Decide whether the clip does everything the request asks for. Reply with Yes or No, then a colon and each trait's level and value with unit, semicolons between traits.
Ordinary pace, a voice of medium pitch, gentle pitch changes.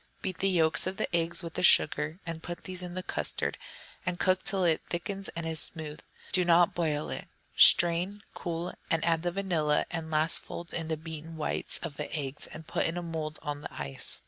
No: fast, 225 wpm; medium, 165 Hz; narrow, 2.0 semitones